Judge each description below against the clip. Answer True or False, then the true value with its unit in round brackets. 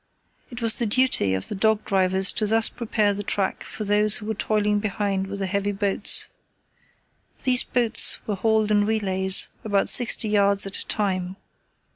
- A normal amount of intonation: False (1.9 semitones)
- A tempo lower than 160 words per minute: False (175 wpm)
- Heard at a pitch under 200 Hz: False (205 Hz)